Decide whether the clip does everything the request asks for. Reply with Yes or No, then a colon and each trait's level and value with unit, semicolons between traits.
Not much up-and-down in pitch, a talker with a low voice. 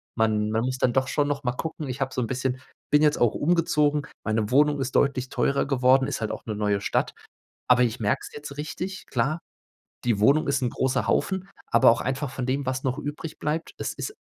No: average, 3.3 semitones; low, 130 Hz